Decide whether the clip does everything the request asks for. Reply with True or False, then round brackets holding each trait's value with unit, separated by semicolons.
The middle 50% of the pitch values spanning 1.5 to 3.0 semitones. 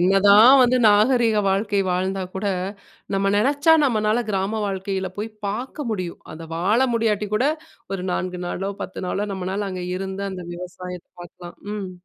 True (2.6 semitones)